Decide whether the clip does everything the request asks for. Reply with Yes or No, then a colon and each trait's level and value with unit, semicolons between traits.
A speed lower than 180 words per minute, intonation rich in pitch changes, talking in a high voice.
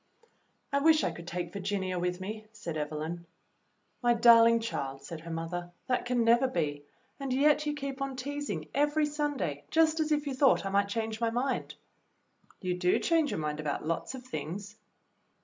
No: average, 185 wpm; wide, 8.0 semitones; high, 225 Hz